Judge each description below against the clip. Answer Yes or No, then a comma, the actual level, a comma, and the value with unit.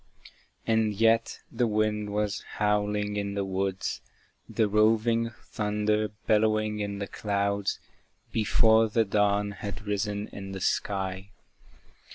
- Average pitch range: No, narrow, 1.2 semitones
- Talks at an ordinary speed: No, slow, 120 wpm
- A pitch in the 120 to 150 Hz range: No, low, 105 Hz